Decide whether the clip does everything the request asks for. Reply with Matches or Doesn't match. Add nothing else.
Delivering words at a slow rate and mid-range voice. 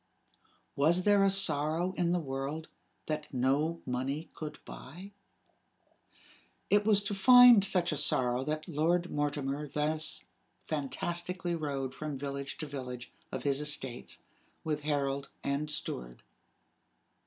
Matches